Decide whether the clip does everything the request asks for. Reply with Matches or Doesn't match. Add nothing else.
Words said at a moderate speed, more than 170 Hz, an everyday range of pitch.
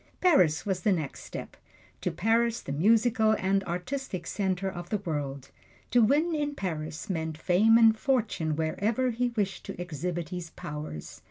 Doesn't match